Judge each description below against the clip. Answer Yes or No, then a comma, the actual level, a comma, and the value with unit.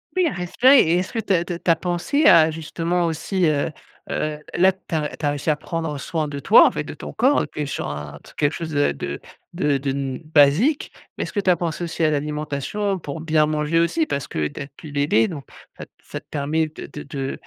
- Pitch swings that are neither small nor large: Yes, average, 3.3 semitones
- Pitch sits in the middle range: Yes, medium, 155 Hz